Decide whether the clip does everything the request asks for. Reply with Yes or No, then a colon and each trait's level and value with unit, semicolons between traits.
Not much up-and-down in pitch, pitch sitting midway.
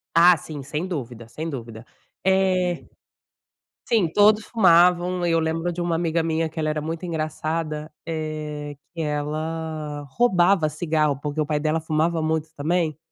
Yes: narrow, 2.2 semitones; medium, 160 Hz